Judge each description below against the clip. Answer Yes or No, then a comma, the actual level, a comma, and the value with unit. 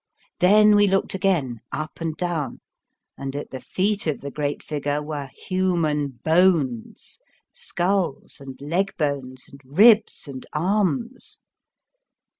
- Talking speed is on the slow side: Yes, slow, 125 wpm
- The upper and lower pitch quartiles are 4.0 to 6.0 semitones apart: Yes, average, 5.2 semitones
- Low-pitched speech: No, medium, 155 Hz